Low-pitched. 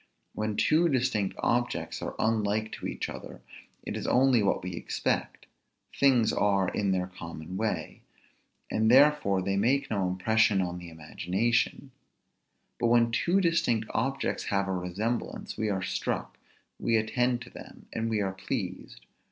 Yes: low, 110 Hz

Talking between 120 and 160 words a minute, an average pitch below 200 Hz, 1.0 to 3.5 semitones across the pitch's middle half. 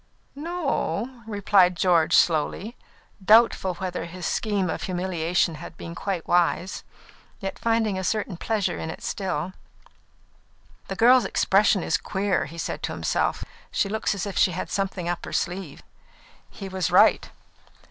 Yes: average, 150 wpm; high, 190 Hz; average, 3.1 semitones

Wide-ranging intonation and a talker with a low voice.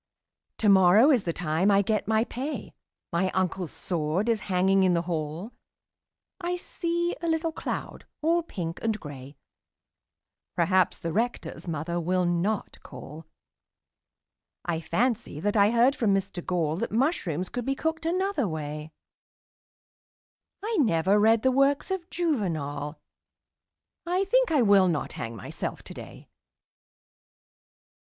No: wide, 7.9 semitones; high, 200 Hz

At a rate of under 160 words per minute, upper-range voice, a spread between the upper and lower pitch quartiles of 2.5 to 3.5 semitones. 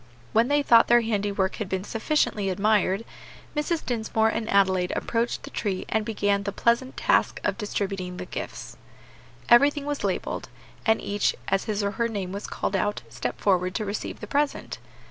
No: average, 175 wpm; high, 210 Hz; average, 3.1 semitones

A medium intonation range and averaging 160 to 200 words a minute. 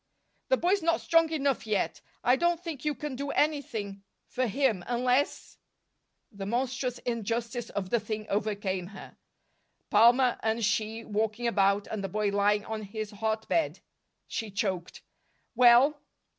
No: average, 4.1 semitones; average, 150 wpm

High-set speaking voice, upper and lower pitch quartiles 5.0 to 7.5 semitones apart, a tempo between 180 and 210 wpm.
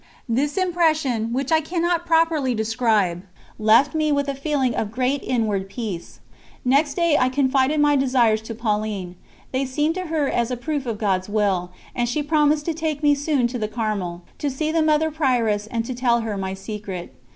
Yes: very high, 255 Hz; wide, 5.5 semitones; average, 190 wpm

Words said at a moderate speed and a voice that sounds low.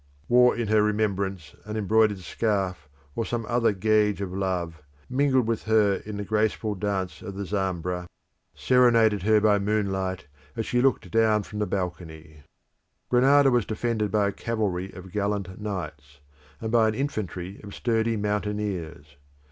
Yes: average, 155 wpm; low, 105 Hz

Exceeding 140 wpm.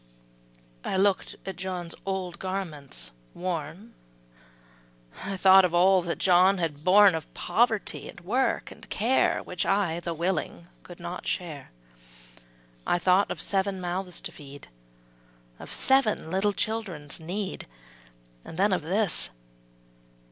No: slow, 135 wpm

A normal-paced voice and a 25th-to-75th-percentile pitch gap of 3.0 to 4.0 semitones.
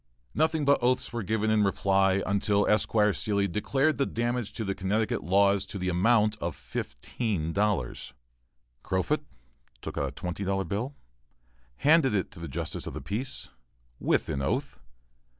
Yes: average, 160 wpm; average, 3.7 semitones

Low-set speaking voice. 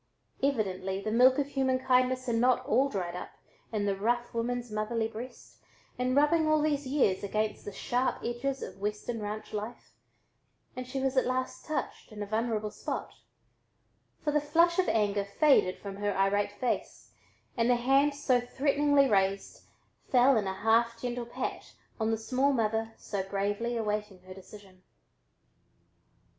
No: high, 235 Hz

